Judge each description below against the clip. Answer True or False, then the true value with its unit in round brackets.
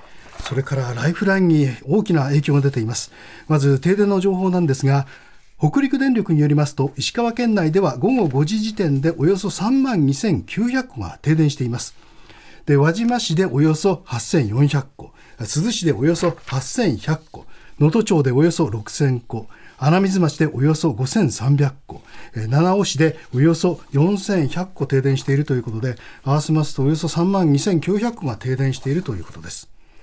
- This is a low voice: False (155 Hz)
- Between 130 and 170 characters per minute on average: False (290 characters per minute)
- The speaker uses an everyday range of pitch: True (5.0 semitones)